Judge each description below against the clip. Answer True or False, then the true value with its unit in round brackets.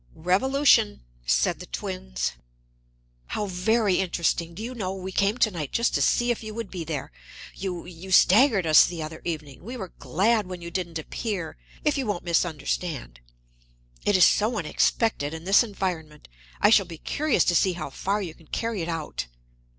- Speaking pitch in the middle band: True (180 Hz)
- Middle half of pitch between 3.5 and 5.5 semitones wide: True (4.7 semitones)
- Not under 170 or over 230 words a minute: True (180 wpm)